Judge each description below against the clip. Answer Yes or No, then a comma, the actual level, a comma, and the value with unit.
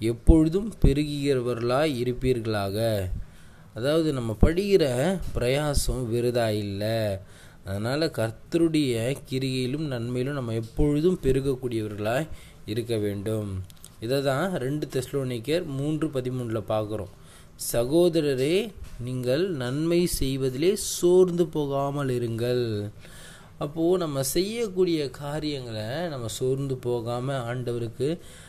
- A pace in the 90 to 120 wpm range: No, average, 80 wpm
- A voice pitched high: No, low, 130 Hz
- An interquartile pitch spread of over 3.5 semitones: Yes, average, 4.8 semitones